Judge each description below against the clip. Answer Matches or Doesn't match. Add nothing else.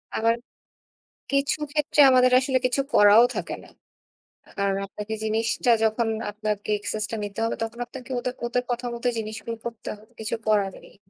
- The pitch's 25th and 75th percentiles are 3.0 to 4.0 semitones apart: Doesn't match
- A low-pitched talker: Doesn't match